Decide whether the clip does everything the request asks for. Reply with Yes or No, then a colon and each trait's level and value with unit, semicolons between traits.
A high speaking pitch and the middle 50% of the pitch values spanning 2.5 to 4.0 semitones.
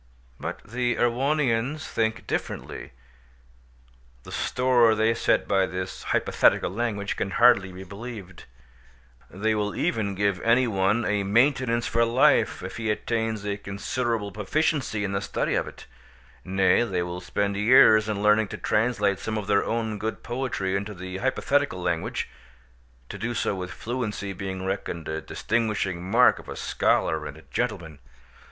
No: low, 105 Hz; average, 3.5 semitones